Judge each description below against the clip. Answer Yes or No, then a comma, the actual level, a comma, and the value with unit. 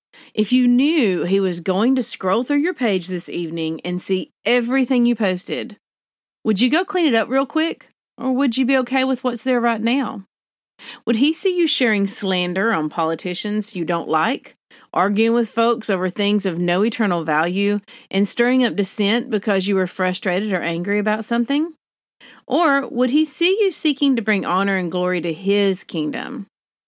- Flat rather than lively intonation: No, wide, 5.5 semitones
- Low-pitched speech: No, high, 215 Hz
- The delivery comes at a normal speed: Yes, average, 185 wpm